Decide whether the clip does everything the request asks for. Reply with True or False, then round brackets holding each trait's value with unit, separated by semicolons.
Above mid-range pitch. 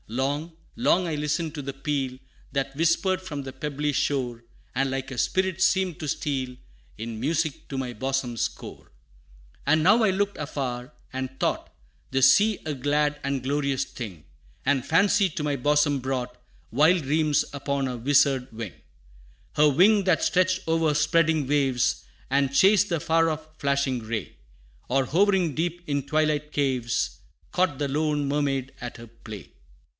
False (145 Hz)